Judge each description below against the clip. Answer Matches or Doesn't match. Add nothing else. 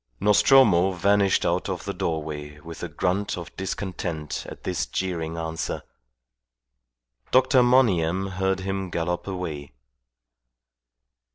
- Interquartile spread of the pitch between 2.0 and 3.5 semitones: Matches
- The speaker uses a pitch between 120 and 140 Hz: Doesn't match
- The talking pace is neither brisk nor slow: Doesn't match